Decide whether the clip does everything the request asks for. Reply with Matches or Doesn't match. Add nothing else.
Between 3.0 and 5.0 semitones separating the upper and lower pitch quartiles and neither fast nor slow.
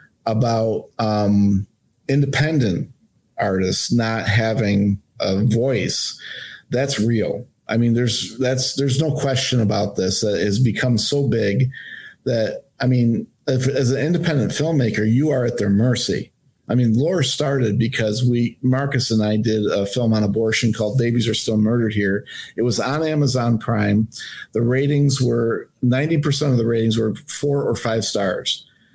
Matches